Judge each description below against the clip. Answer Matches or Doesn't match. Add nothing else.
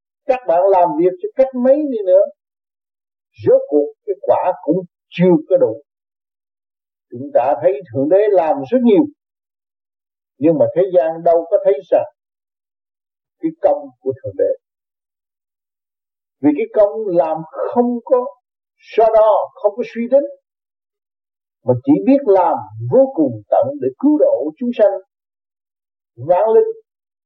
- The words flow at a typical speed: Doesn't match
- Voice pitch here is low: Doesn't match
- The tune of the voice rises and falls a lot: Matches